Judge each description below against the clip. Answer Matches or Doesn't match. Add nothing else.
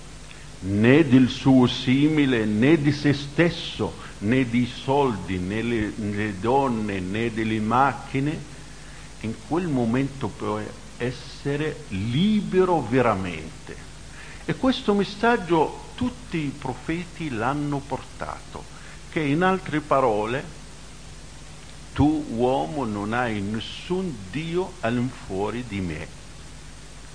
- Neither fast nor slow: Doesn't match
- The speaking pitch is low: Matches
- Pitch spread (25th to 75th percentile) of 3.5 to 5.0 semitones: Doesn't match